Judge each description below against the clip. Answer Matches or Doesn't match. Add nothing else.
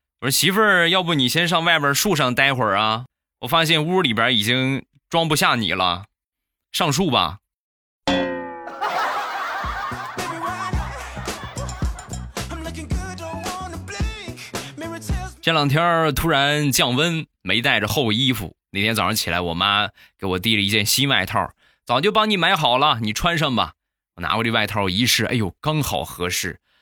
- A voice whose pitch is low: Matches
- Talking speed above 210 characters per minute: Doesn't match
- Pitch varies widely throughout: Matches